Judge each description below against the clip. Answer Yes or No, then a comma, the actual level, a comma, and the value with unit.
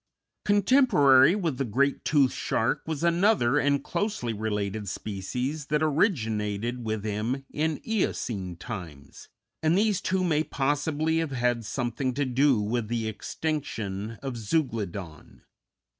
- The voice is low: Yes, low, 130 Hz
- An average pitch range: No, wide, 6.2 semitones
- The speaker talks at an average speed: No, slow, 130 wpm